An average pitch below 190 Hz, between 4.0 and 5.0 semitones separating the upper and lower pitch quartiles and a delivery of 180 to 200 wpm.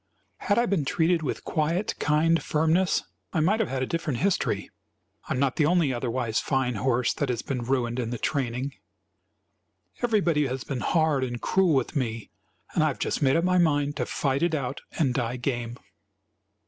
Yes: medium, 140 Hz; average, 4.7 semitones; average, 190 wpm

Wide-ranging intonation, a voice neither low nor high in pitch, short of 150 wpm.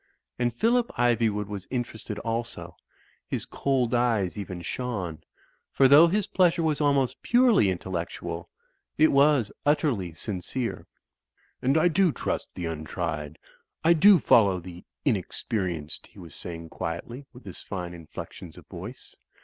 No: wide, 8.0 semitones; low, 115 Hz; average, 140 wpm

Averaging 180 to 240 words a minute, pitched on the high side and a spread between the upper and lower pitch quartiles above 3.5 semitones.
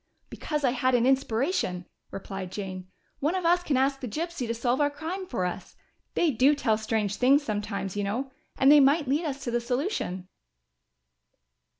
Yes: average, 185 wpm; very high, 255 Hz; wide, 5.4 semitones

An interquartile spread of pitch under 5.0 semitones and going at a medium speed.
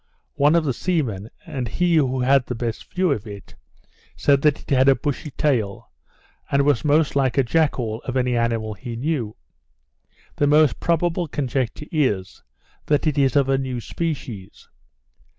Yes: average, 4.1 semitones; average, 170 wpm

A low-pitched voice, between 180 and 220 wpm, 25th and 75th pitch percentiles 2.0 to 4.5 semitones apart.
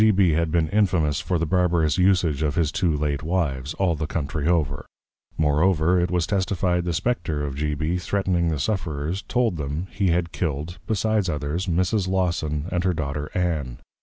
Yes: very low, 85 Hz; average, 195 wpm; average, 3.5 semitones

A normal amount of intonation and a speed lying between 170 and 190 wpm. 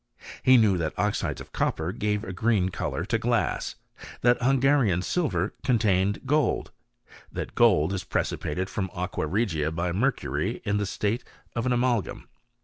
No: average, 5.0 semitones; average, 150 wpm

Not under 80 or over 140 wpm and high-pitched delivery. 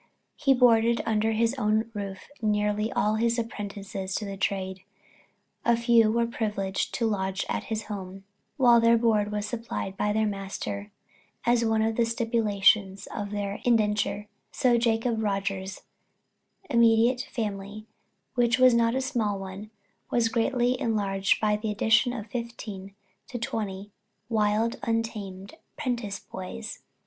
Yes: slow, 135 wpm; high, 215 Hz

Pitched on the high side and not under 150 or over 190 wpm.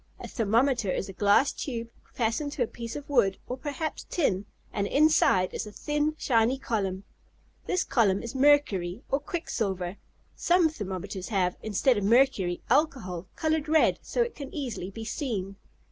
Yes: high, 230 Hz; average, 160 wpm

